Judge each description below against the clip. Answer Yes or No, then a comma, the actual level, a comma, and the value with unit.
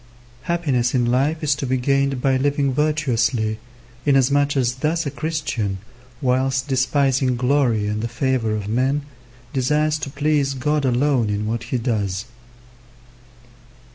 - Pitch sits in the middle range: No, low, 130 Hz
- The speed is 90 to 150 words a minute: Yes, average, 140 wpm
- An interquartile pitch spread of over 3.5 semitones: No, average, 3.0 semitones